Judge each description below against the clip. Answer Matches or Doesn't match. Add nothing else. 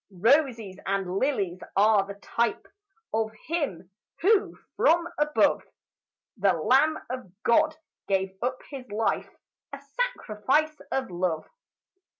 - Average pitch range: Doesn't match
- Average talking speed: Doesn't match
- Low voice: Doesn't match